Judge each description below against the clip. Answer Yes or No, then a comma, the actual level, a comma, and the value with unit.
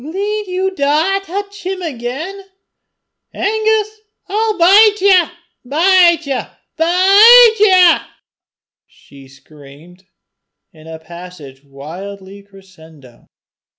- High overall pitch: Yes, very high, 330 Hz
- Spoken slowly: Yes, slow, 95 wpm